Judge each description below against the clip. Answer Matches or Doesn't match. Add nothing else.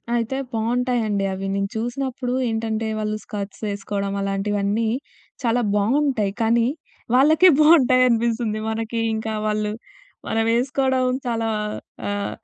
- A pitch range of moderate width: Matches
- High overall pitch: Matches